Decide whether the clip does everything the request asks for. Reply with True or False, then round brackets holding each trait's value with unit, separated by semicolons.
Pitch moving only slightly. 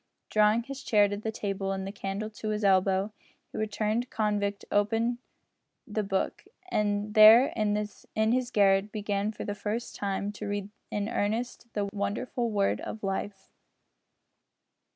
True (1.4 semitones)